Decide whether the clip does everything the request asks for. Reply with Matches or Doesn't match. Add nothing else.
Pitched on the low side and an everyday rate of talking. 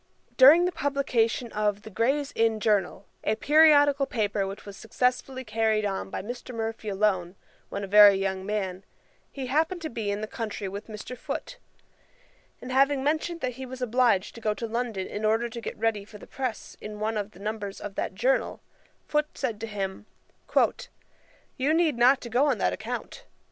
Doesn't match